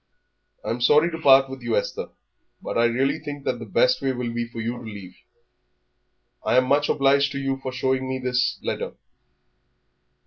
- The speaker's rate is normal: Yes, average, 185 wpm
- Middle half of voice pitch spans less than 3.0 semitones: Yes, narrow, 2.5 semitones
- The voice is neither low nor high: No, low, 130 Hz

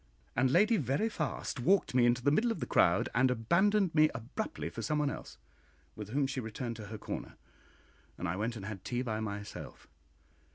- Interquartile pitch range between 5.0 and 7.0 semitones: Yes, wide, 5.6 semitones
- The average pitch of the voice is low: Yes, low, 125 Hz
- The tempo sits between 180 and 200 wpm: Yes, average, 190 wpm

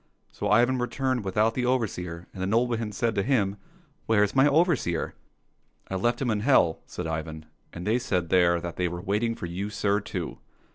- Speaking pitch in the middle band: No, low, 105 Hz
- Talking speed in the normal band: No, fast, 225 wpm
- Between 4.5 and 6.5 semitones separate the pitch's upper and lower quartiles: Yes, average, 5.3 semitones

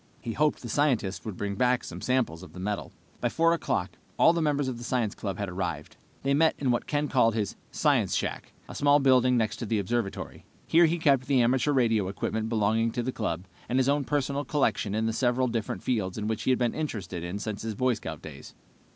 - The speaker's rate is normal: No, fast, 230 wpm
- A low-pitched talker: Yes, low, 120 Hz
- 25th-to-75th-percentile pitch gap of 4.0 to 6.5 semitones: Yes, average, 4.7 semitones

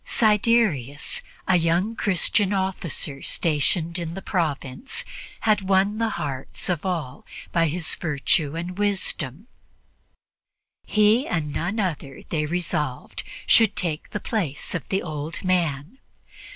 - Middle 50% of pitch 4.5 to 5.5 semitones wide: Yes, average, 4.9 semitones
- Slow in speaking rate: Yes, slow, 125 wpm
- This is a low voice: No, medium, 175 Hz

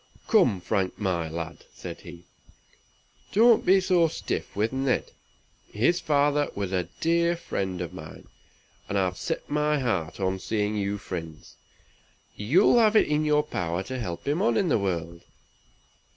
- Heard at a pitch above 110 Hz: No, low, 105 Hz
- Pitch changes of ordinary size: No, wide, 8.7 semitones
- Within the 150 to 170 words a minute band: Yes, average, 155 wpm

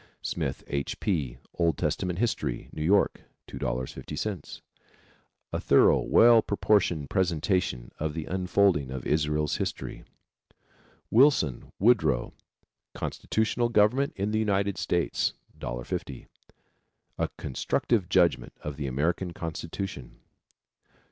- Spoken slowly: Yes, slow, 100 wpm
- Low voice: Yes, very low, 90 Hz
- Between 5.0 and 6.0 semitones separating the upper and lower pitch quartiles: Yes, wide, 5.5 semitones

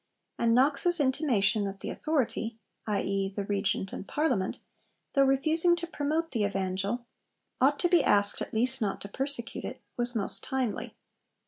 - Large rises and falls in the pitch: Yes, wide, 6.0 semitones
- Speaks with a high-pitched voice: Yes, high, 240 Hz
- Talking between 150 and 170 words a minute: Yes, average, 155 wpm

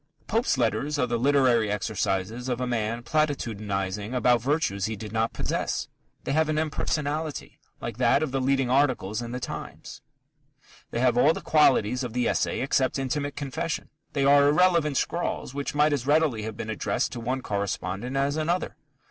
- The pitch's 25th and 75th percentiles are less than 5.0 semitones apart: Yes, average, 4.5 semitones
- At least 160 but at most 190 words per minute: Yes, average, 175 wpm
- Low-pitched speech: Yes, low, 130 Hz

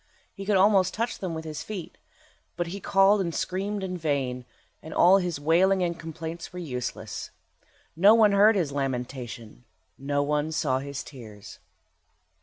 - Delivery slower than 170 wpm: Yes, average, 160 wpm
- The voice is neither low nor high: Yes, medium, 165 Hz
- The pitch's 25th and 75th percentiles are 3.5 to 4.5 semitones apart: No, wide, 5.4 semitones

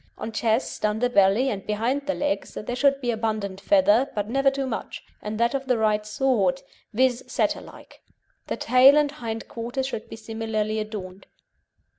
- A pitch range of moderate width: Yes, average, 3.7 semitones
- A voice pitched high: Yes, high, 225 Hz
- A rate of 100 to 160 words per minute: No, average, 175 wpm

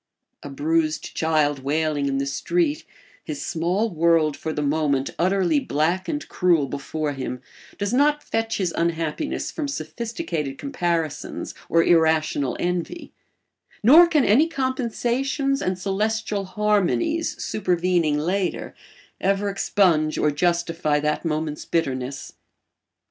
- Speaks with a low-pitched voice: No, medium, 170 Hz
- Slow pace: Yes, slow, 120 wpm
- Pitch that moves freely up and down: Yes, wide, 6.2 semitones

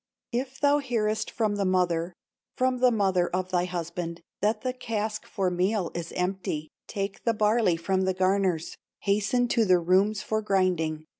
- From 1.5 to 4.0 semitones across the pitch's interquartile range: Yes, average, 3.4 semitones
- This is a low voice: No, high, 195 Hz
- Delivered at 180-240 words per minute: No, average, 165 wpm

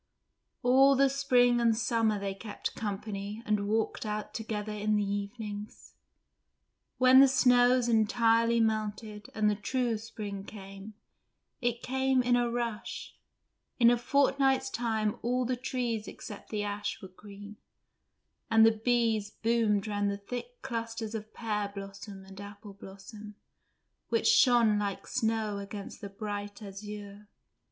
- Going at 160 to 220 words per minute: No, average, 140 wpm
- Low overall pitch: No, high, 220 Hz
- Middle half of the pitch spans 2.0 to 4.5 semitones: Yes, average, 2.7 semitones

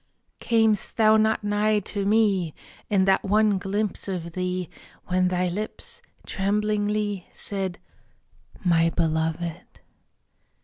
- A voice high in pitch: Yes, high, 195 Hz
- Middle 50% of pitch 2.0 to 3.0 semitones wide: Yes, average, 2.7 semitones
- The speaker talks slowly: Yes, slow, 105 wpm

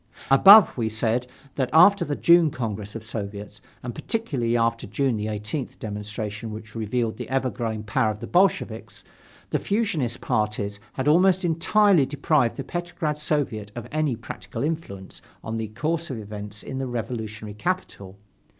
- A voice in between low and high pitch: No, low, 120 Hz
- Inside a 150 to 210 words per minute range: Yes, average, 160 wpm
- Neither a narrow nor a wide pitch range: No, wide, 6.2 semitones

